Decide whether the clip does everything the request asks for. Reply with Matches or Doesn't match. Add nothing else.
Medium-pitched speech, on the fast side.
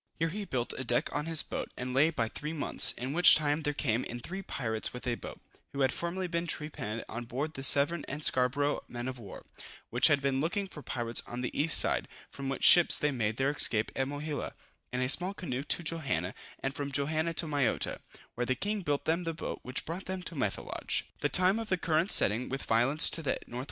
Matches